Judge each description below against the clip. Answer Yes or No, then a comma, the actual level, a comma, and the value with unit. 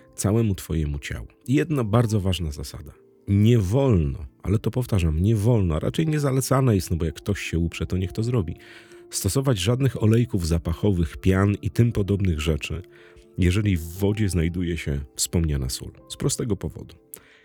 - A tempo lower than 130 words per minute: No, fast, 160 wpm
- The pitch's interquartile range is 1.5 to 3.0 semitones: No, wide, 5.5 semitones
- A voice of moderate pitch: No, low, 100 Hz